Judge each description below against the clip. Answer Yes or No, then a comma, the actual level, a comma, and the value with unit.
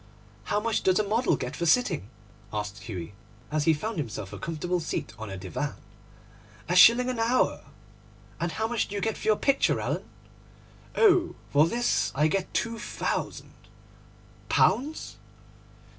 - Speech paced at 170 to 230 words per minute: No, average, 160 wpm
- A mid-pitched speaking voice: Yes, medium, 180 Hz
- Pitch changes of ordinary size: No, wide, 7.7 semitones